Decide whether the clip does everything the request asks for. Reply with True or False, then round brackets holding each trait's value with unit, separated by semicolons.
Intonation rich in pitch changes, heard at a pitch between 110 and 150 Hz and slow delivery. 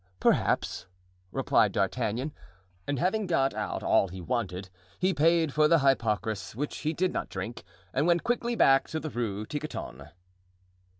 False (6.8 semitones; 140 Hz; 155 wpm)